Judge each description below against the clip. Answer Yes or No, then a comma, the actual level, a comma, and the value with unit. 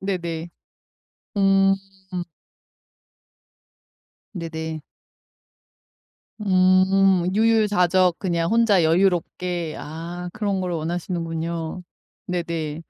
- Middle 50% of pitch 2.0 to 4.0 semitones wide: Yes, average, 2.7 semitones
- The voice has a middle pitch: Yes, medium, 180 Hz